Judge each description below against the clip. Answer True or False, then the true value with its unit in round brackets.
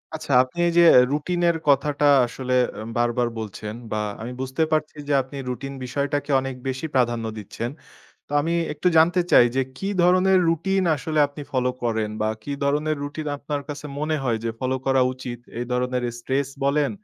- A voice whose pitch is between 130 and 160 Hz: True (140 Hz)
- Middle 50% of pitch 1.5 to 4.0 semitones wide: True (3.5 semitones)